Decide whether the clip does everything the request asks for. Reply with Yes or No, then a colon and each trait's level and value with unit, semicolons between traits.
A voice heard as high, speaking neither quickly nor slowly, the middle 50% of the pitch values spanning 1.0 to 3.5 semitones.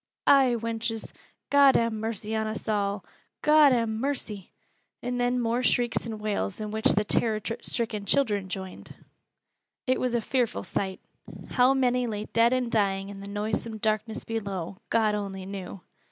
Yes: high, 220 Hz; average, 160 wpm; average, 2.9 semitones